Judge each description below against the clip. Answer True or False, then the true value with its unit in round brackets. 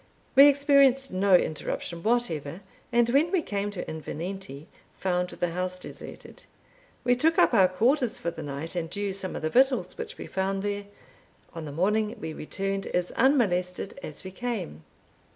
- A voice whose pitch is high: True (195 Hz)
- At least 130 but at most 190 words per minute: True (170 wpm)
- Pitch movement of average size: False (5.8 semitones)